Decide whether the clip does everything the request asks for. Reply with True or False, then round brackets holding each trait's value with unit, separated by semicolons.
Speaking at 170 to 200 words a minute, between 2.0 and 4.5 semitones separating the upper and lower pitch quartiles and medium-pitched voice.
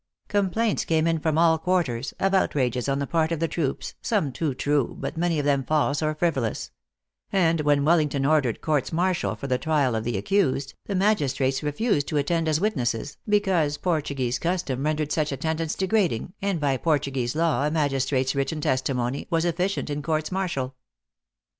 True (185 wpm; 3.7 semitones; 150 Hz)